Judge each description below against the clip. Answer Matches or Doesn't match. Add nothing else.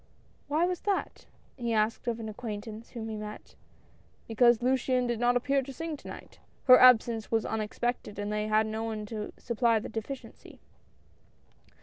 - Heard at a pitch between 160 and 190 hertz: Doesn't match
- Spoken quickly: Doesn't match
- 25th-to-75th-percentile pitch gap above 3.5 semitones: Doesn't match